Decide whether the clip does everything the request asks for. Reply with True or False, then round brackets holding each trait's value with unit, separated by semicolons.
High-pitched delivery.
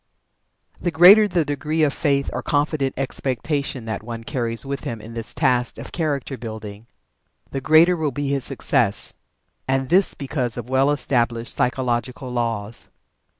False (135 Hz)